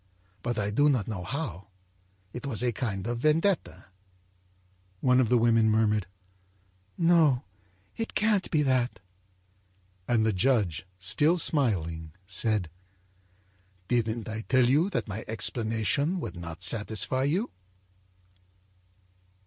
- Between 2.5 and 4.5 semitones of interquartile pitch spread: No, average, 5.3 semitones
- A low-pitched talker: Yes, low, 115 Hz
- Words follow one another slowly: Yes, slow, 115 wpm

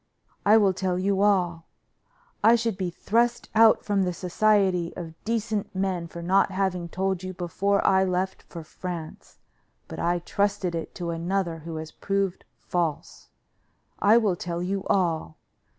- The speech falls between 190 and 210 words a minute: No, average, 155 wpm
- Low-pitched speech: No, medium, 185 Hz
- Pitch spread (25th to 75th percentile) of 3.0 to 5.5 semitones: No, narrow, 2.5 semitones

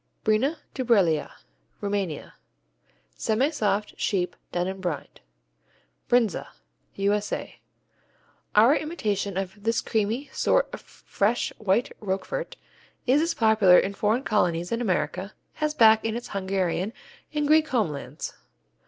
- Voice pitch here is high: Yes, high, 210 Hz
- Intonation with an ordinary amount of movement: Yes, average, 4.2 semitones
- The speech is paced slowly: Yes, slow, 115 wpm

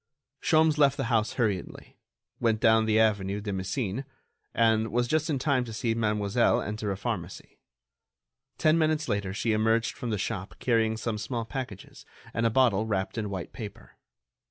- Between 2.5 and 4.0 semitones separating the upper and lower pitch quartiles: Yes, average, 2.9 semitones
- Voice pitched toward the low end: Yes, low, 110 Hz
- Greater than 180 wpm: No, average, 170 wpm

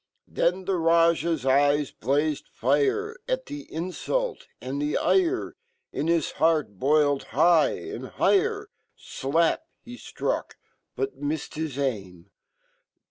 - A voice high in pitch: No, medium, 160 Hz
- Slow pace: Yes, slow, 95 wpm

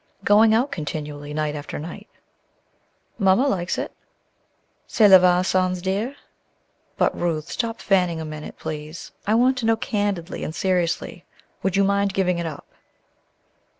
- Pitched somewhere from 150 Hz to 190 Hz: Yes, medium, 185 Hz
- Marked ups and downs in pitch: No, average, 4.3 semitones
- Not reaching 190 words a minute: Yes, average, 145 wpm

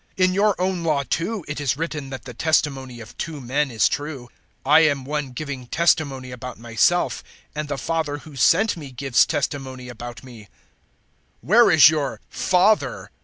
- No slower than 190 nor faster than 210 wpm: No, average, 180 wpm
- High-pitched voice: No, medium, 145 Hz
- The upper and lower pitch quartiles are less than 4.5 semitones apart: Yes, average, 4.1 semitones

